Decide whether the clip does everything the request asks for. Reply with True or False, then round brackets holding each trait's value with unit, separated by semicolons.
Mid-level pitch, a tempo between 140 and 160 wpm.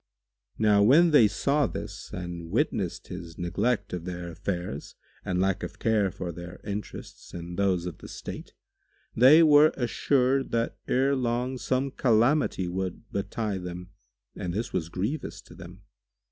False (100 Hz; 150 wpm)